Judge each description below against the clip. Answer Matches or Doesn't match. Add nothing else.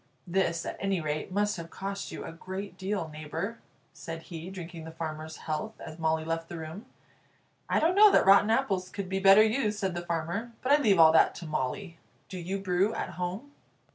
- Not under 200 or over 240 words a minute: Matches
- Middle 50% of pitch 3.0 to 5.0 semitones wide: Matches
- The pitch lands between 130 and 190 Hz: Matches